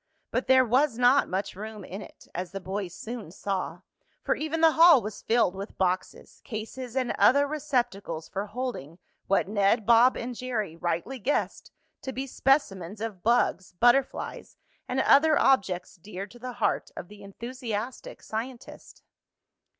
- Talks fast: No, average, 155 wpm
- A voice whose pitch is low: No, high, 225 Hz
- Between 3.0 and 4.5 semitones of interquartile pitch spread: No, average, 4.9 semitones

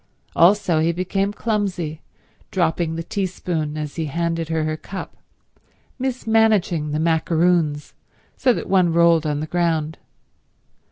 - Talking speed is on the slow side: Yes, slow, 125 wpm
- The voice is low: No, medium, 170 Hz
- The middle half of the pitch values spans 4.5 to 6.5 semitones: No, average, 3.1 semitones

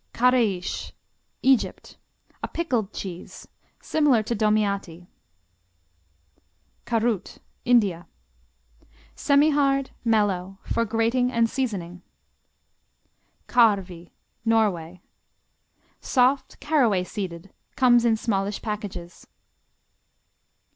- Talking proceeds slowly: Yes, slow, 70 wpm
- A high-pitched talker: Yes, high, 220 Hz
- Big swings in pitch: No, average, 4.5 semitones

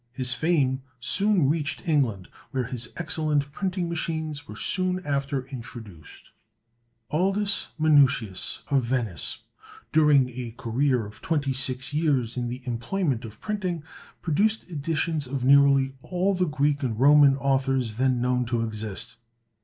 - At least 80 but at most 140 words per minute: Yes, slow, 135 wpm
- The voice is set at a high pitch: No, medium, 140 Hz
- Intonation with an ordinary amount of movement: Yes, average, 4.2 semitones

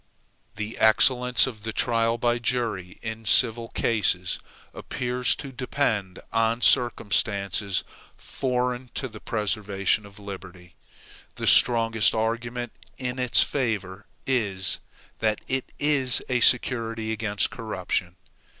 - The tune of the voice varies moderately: Yes, average, 3.2 semitones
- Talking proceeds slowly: Yes, slow, 115 wpm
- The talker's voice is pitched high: No, low, 115 Hz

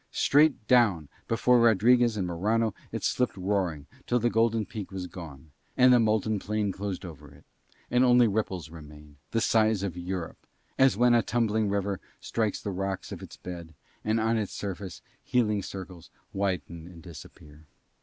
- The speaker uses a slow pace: No, average, 165 wpm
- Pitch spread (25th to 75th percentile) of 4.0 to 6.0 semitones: Yes, average, 4.5 semitones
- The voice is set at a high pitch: No, low, 100 Hz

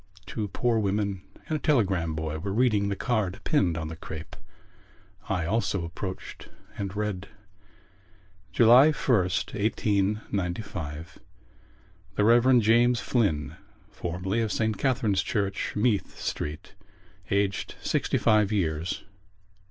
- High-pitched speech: No, low, 100 Hz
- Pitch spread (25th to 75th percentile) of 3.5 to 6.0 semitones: Yes, average, 4.0 semitones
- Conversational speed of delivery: No, slow, 115 wpm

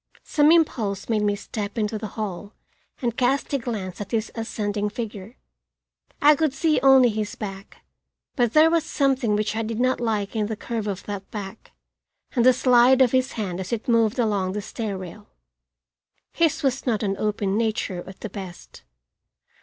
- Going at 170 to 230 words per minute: Yes, average, 180 wpm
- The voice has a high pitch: Yes, high, 220 Hz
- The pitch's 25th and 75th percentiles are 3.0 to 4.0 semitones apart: Yes, average, 3.6 semitones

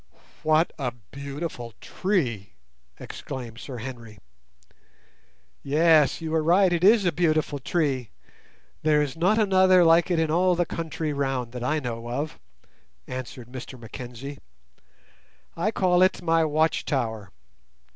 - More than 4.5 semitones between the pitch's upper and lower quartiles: Yes, average, 5.2 semitones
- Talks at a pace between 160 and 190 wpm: No, slow, 135 wpm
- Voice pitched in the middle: Yes, medium, 150 Hz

